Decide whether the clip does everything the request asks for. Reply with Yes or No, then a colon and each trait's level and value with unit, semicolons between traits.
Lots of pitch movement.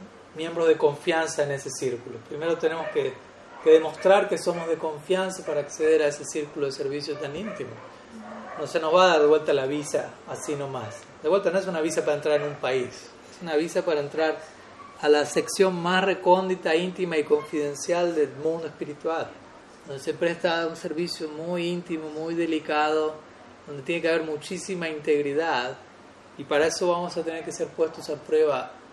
No: average, 2.9 semitones